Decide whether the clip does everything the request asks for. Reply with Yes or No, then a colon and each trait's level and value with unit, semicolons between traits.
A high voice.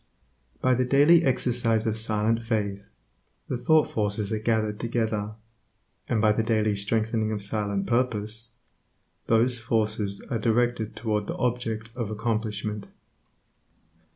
No: low, 110 Hz